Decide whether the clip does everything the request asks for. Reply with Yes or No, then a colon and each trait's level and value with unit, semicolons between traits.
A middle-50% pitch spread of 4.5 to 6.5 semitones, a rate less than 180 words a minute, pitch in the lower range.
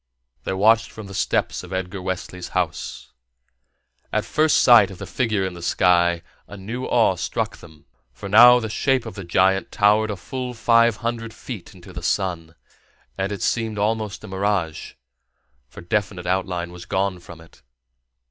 No: average, 3.5 semitones; average, 170 wpm; low, 100 Hz